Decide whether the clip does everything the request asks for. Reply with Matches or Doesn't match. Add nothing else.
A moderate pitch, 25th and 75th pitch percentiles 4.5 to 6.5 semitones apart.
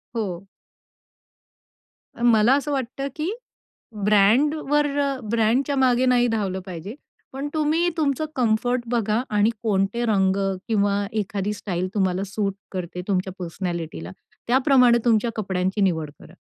Doesn't match